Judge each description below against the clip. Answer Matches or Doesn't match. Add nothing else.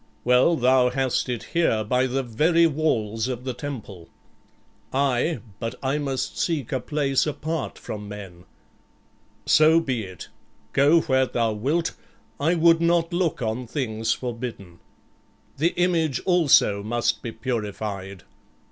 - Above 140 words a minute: Doesn't match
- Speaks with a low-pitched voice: Matches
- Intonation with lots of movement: Matches